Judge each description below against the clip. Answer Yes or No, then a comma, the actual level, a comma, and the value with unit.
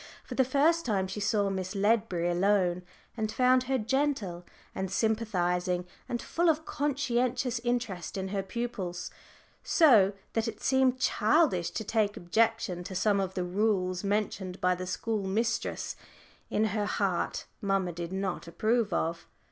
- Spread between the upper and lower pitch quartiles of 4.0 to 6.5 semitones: Yes, average, 4.4 semitones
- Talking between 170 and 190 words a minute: No, average, 155 wpm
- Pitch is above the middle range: Yes, high, 205 Hz